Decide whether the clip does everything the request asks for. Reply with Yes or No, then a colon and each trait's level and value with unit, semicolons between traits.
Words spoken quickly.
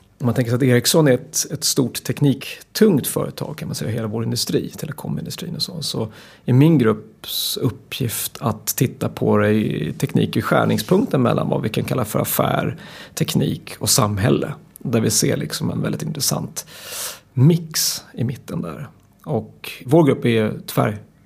No: average, 165 wpm